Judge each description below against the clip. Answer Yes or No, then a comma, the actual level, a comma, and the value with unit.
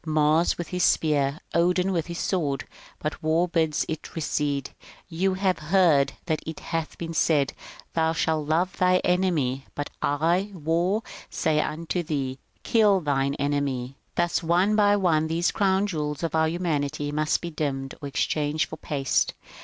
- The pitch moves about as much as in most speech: Yes, average, 3.3 semitones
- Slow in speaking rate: No, average, 170 wpm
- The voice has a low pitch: No, medium, 160 Hz